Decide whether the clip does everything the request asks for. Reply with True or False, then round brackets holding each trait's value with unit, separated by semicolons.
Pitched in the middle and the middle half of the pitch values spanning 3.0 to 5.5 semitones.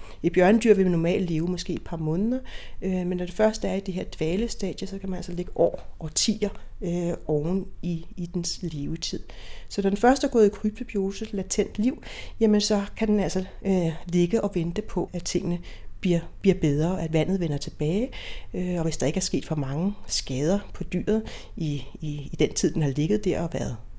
True (180 Hz; 3.6 semitones)